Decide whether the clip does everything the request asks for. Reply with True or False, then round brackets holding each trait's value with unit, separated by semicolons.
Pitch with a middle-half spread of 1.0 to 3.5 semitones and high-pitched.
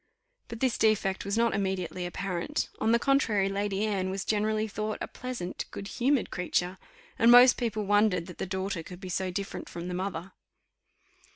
True (2.9 semitones; 200 Hz)